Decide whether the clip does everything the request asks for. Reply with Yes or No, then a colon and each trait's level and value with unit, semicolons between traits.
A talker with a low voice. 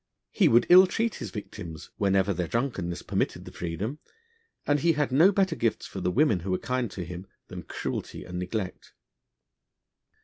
Yes: low, 105 Hz